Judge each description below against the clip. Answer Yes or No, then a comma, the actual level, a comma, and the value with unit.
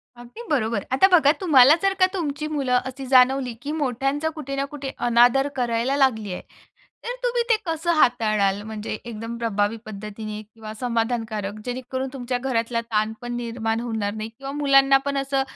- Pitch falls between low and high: No, very high, 250 Hz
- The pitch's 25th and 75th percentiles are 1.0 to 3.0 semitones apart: No, average, 3.7 semitones